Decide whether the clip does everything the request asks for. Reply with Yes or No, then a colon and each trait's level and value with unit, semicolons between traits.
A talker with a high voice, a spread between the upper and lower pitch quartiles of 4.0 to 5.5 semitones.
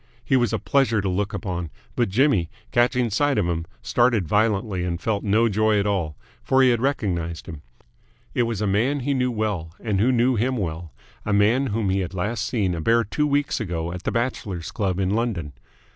No: low, 105 Hz; average, 4.7 semitones